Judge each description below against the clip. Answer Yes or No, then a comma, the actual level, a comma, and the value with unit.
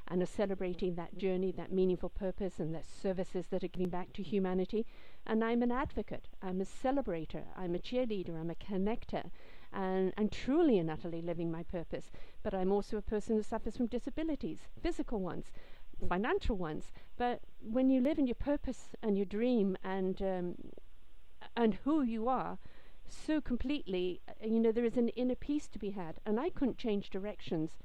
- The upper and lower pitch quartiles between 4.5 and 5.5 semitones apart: Yes, average, 4.8 semitones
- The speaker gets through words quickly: No, average, 185 wpm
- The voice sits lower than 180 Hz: No, high, 200 Hz